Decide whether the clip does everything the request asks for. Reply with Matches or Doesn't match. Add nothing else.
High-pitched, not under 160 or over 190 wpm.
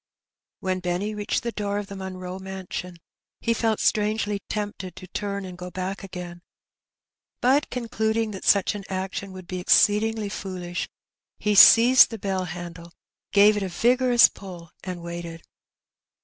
Doesn't match